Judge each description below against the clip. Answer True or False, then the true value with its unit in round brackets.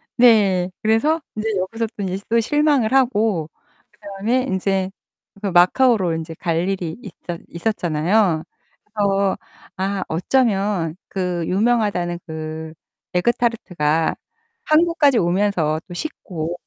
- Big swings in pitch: False (4.5 semitones)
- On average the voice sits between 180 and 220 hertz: True (195 Hz)